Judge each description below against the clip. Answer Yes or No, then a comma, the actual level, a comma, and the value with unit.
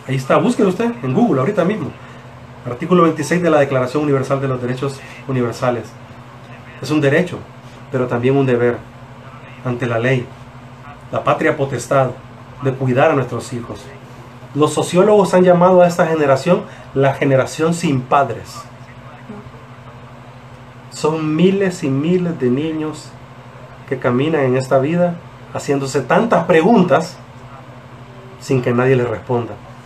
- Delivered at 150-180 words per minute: No, average, 135 wpm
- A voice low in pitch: Yes, low, 130 Hz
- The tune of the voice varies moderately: Yes, average, 3.4 semitones